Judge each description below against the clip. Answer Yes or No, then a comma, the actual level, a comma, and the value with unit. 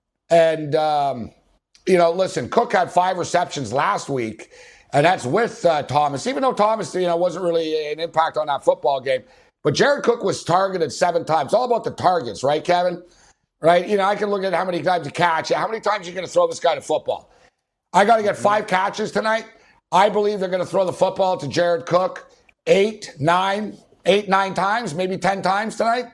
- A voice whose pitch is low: No, medium, 185 Hz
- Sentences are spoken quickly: Yes, fast, 215 wpm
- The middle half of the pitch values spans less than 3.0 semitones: No, average, 3.6 semitones